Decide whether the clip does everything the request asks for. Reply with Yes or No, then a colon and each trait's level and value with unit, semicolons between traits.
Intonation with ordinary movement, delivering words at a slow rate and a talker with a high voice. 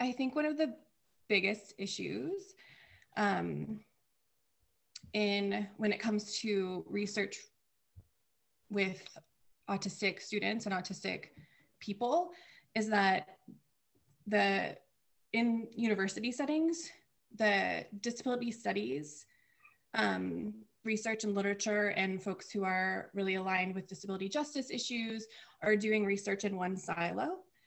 Yes: average, 3.4 semitones; slow, 105 wpm; high, 205 Hz